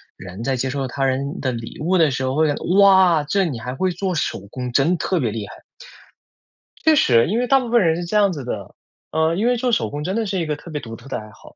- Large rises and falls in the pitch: Yes, wide, 6.6 semitones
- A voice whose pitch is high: No, medium, 155 Hz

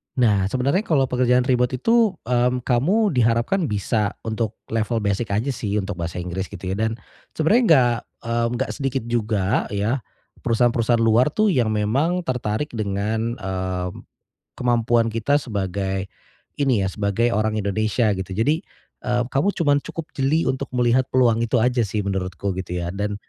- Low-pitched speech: Yes, low, 115 Hz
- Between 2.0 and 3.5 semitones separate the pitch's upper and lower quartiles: No, average, 4.2 semitones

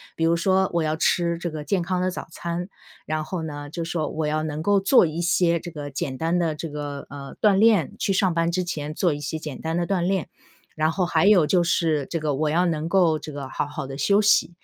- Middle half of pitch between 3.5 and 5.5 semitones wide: No, average, 2.8 semitones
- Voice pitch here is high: No, medium, 165 Hz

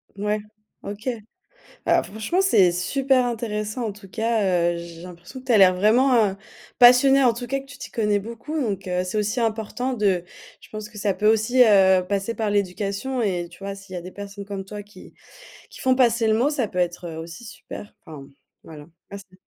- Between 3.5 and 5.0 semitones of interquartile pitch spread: Yes, average, 4.0 semitones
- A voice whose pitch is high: Yes, high, 210 Hz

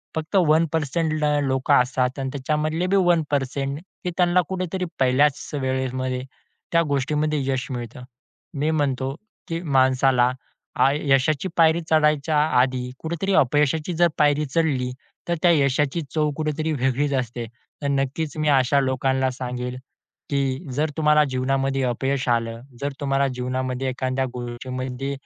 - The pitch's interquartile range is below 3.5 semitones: Yes, average, 3.0 semitones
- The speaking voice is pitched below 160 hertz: Yes, medium, 140 Hz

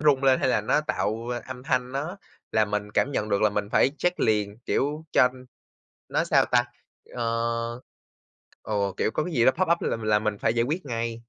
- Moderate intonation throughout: Yes, average, 4.7 semitones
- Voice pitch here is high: No, low, 120 Hz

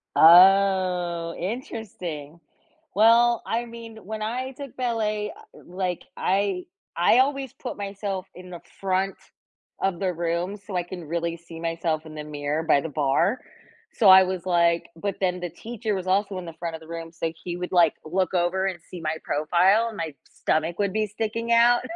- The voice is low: No, medium, 185 Hz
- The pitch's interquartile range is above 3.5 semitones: Yes, average, 4.2 semitones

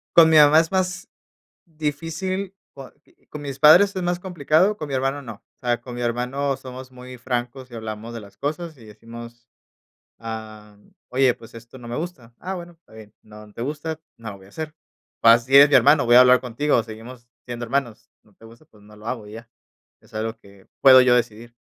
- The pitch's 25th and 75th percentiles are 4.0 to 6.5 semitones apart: Yes, average, 4.7 semitones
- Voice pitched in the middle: No, low, 125 Hz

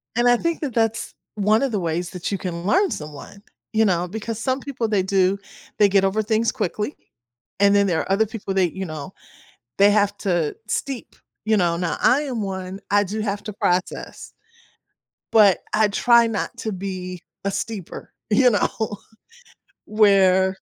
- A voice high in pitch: Yes, high, 200 Hz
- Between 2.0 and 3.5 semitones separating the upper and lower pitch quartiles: Yes, average, 2.9 semitones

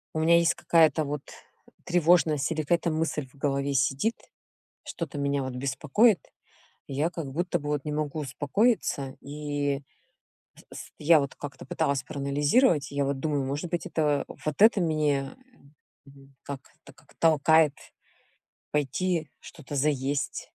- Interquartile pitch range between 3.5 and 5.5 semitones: No, narrow, 2.6 semitones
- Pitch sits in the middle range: Yes, medium, 145 Hz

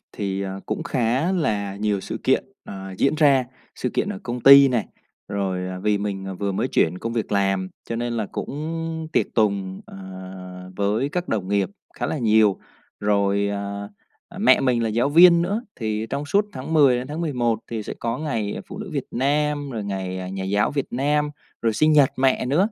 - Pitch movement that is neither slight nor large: No, wide, 6.1 semitones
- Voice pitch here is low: Yes, low, 115 Hz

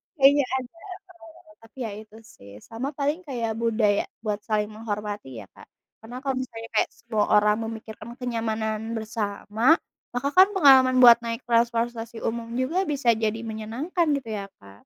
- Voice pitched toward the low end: No, high, 230 Hz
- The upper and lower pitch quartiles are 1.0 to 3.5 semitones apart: Yes, average, 3.0 semitones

